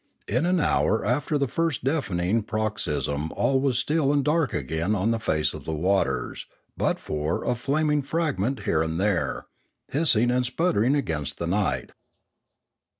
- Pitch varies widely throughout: Yes, wide, 8.5 semitones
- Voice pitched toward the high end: No, low, 115 Hz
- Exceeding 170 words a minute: No, average, 155 wpm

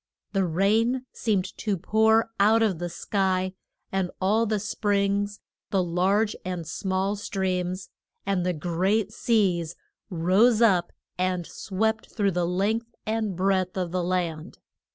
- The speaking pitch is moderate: No, high, 195 Hz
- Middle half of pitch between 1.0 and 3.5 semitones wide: Yes, average, 2.8 semitones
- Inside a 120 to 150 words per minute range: Yes, slow, 135 wpm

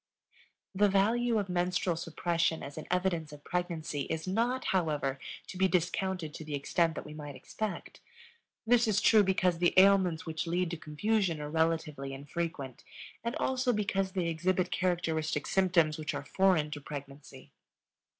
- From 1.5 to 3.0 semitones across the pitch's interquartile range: No, average, 3.7 semitones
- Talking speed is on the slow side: No, average, 160 wpm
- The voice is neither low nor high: Yes, medium, 170 Hz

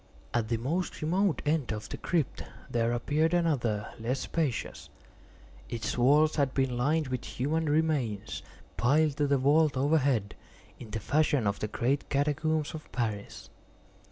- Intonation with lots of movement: No, average, 4.7 semitones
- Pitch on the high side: No, medium, 140 Hz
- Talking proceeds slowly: No, average, 150 wpm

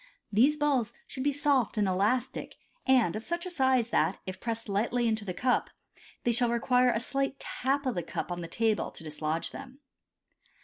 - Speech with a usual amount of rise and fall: Yes, average, 4.1 semitones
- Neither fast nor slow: Yes, average, 190 wpm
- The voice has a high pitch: Yes, high, 240 Hz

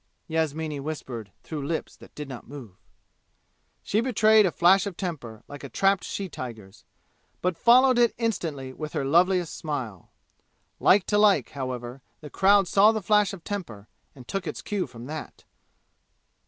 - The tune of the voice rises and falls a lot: Yes, wide, 6.9 semitones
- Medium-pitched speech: Yes, medium, 160 Hz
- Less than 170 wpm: Yes, average, 160 wpm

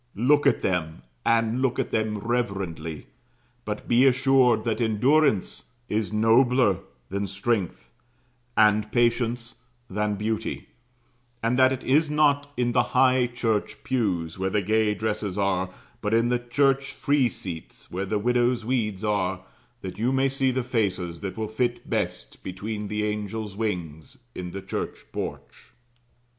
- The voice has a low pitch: Yes, low, 110 Hz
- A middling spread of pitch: Yes, average, 3.7 semitones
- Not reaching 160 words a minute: Yes, average, 150 wpm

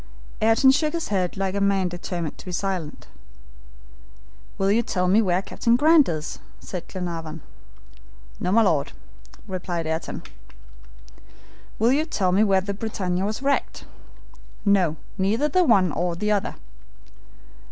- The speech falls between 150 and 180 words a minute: No, average, 140 wpm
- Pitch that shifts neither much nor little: Yes, average, 3.9 semitones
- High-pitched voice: Yes, high, 195 Hz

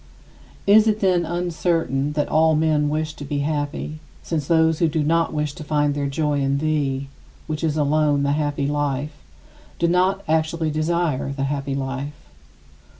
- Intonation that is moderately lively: No, narrow, 2.0 semitones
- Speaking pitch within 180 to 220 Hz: No, medium, 150 Hz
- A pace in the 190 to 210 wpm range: No, average, 165 wpm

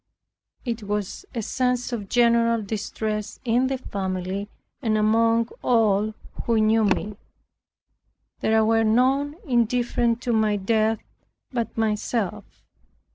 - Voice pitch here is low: No, high, 225 Hz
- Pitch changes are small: Yes, narrow, 2.0 semitones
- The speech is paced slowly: Yes, slow, 115 wpm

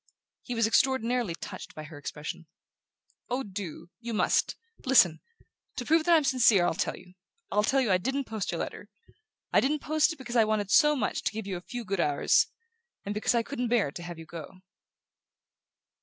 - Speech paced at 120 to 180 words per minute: No, average, 190 wpm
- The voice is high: Yes, high, 225 Hz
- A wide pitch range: Yes, wide, 6.5 semitones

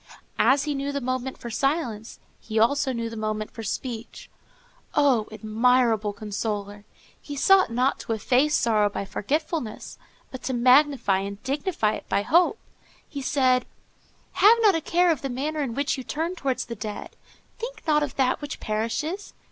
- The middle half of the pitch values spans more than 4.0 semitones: Yes, average, 4.9 semitones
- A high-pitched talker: Yes, very high, 255 Hz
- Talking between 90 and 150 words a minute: No, average, 165 wpm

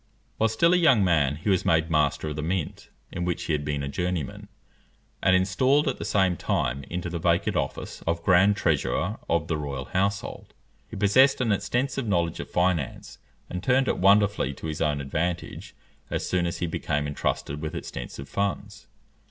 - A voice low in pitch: Yes, very low, 90 Hz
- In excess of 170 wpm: Yes, average, 185 wpm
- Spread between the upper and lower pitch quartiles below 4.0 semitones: No, average, 4.7 semitones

